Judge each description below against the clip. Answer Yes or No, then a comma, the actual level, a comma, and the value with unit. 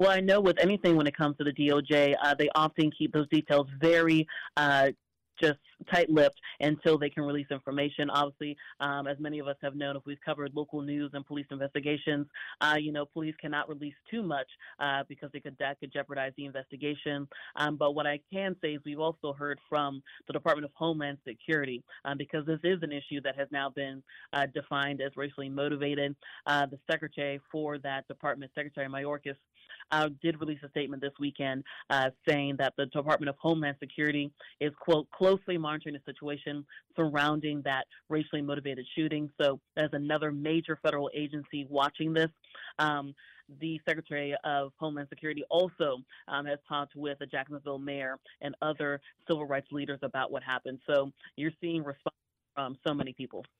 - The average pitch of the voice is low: No, medium, 145 Hz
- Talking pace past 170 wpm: Yes, average, 185 wpm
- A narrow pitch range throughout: Yes, narrow, 1.6 semitones